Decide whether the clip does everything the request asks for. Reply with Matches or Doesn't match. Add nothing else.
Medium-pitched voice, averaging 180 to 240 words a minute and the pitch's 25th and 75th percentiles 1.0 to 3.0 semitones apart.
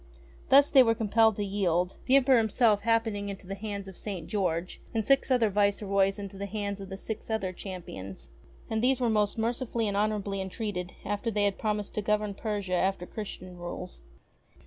Doesn't match